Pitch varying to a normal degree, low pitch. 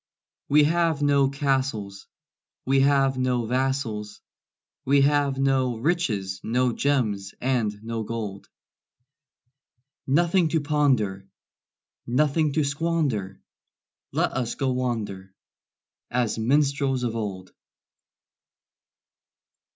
Yes: average, 4.4 semitones; low, 130 Hz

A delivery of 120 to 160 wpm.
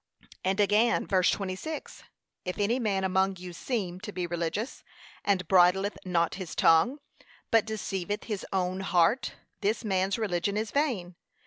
Yes: average, 145 wpm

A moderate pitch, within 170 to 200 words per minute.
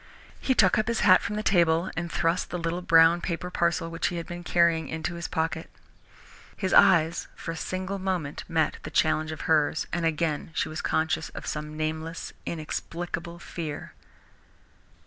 Yes: medium, 165 Hz; average, 175 wpm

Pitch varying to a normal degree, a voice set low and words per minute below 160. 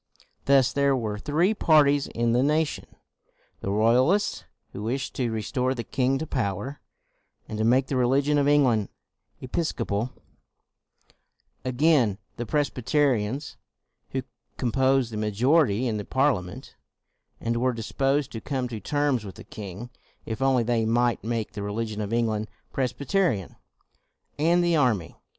Yes: average, 4.1 semitones; low, 125 Hz; average, 145 wpm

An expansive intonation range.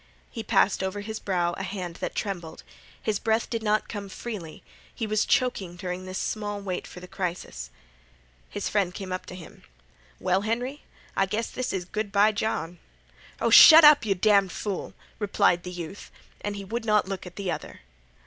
No: average, 2.9 semitones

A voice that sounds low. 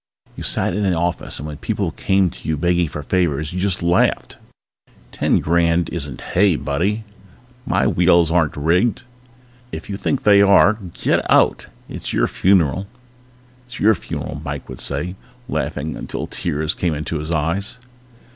Yes: very low, 85 Hz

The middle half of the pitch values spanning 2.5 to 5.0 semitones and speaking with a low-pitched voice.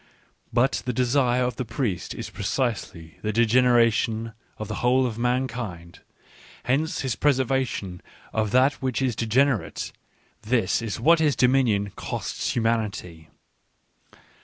Yes: average, 3.2 semitones; low, 120 Hz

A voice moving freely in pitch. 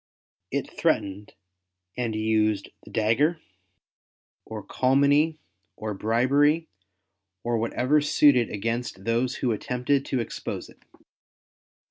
No: average, 4.4 semitones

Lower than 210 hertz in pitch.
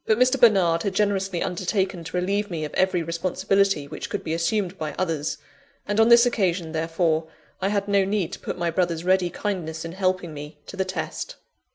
Yes: medium, 185 Hz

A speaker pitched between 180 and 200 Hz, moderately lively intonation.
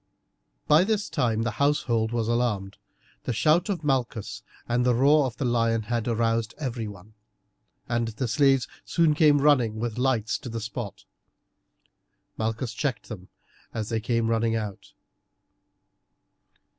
No: low, 120 Hz; average, 3.3 semitones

